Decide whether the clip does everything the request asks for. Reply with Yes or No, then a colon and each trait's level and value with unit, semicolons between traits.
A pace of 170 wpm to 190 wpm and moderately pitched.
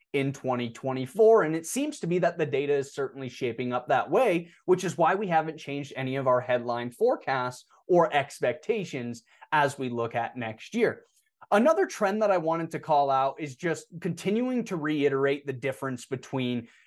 Yes: average, 180 wpm; medium, 145 Hz